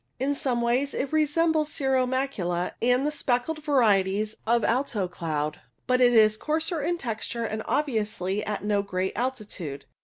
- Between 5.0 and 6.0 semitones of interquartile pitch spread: Yes, average, 5.3 semitones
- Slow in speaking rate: No, average, 155 wpm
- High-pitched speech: Yes, high, 240 Hz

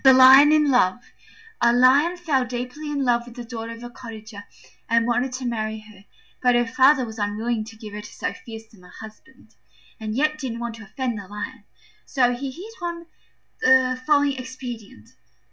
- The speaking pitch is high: Yes, high, 240 Hz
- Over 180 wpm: Yes, average, 190 wpm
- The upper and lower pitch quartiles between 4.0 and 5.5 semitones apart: No, average, 3.1 semitones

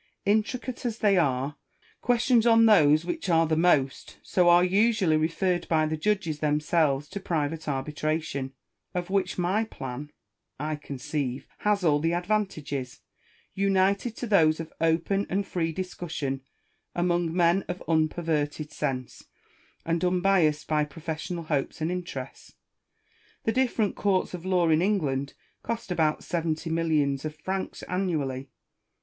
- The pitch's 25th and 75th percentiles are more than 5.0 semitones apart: No, average, 4.0 semitones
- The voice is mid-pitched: Yes, medium, 165 Hz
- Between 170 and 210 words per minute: No, average, 140 wpm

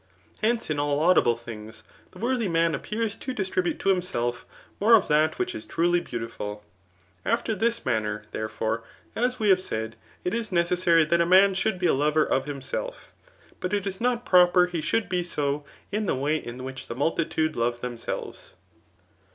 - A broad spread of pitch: Yes, wide, 7.5 semitones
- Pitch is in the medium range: Yes, medium, 170 Hz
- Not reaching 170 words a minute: No, average, 180 wpm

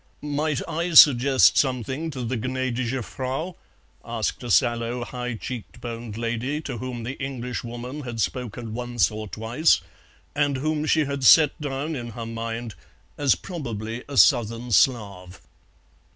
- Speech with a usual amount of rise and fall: Yes, average, 3.2 semitones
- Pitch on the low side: Yes, low, 125 Hz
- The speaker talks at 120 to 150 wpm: Yes, average, 140 wpm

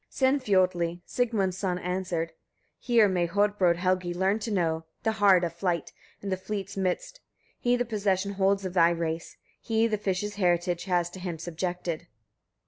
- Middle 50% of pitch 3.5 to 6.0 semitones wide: No, average, 2.9 semitones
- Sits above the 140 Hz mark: Yes, medium, 185 Hz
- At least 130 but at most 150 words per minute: No, average, 165 wpm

